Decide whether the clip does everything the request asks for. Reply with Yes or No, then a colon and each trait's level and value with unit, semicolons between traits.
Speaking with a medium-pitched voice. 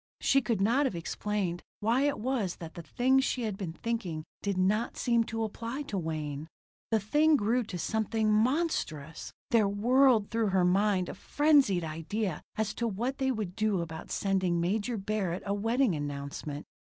No: high, 210 Hz